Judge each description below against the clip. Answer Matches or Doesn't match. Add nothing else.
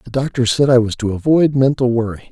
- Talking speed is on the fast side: Matches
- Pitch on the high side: Doesn't match